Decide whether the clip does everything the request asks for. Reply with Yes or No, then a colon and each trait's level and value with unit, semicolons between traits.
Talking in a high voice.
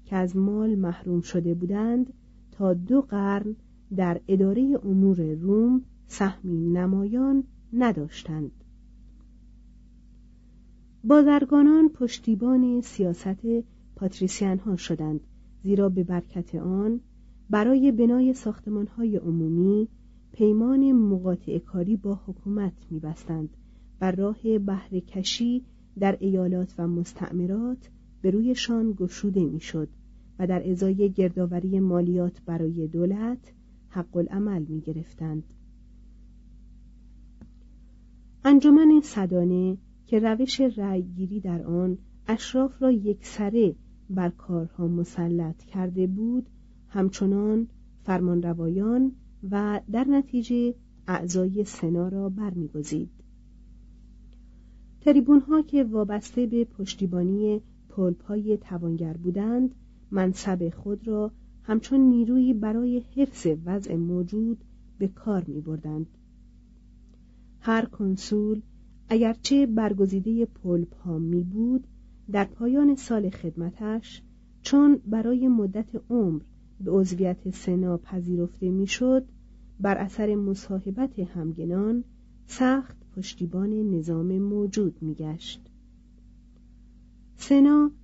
Yes: high, 200 Hz